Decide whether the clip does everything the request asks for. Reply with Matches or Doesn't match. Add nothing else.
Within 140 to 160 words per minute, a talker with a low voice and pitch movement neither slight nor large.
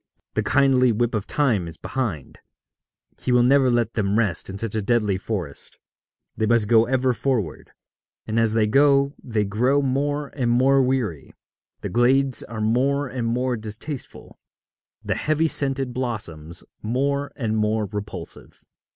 Matches